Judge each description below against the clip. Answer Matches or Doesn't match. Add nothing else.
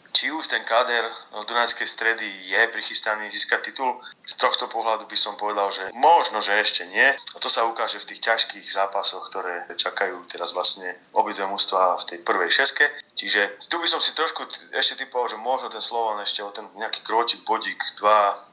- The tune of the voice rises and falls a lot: Doesn't match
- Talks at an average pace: Doesn't match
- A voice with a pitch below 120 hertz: Matches